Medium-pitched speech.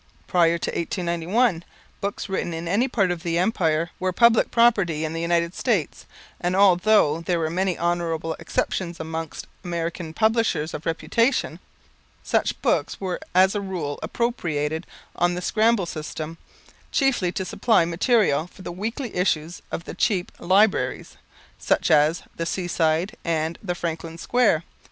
Yes: medium, 175 Hz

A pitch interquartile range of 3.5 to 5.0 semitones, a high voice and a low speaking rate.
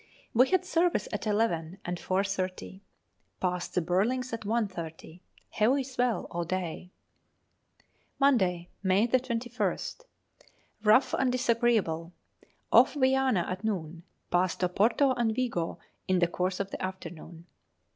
No: wide, 5.4 semitones; high, 200 Hz; slow, 120 wpm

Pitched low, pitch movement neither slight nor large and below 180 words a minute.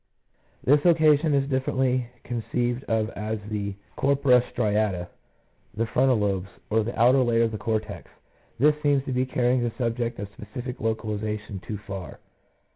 Yes: low, 115 Hz; average, 3.4 semitones; average, 155 wpm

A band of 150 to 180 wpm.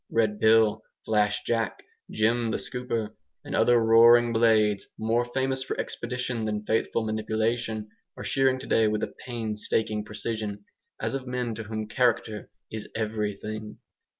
No: average, 140 wpm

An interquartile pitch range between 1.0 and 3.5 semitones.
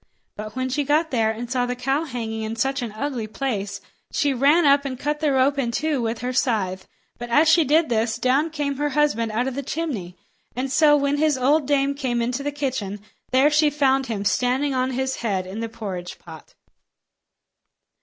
No: average, 4.1 semitones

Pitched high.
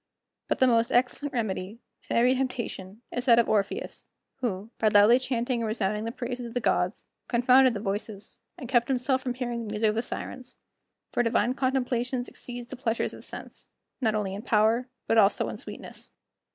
Yes: high, 235 Hz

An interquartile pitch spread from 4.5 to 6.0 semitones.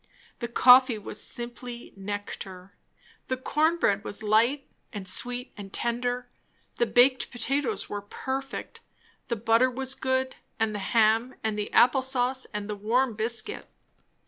No: average, 3.5 semitones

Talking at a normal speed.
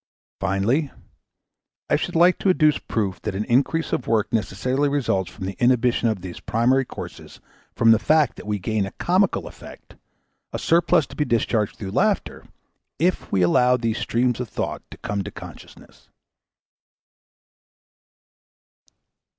Yes: average, 150 wpm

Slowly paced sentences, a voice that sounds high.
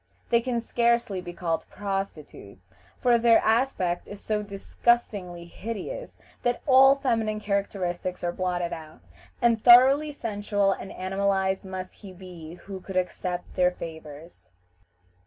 Yes: slow, 130 wpm; high, 195 Hz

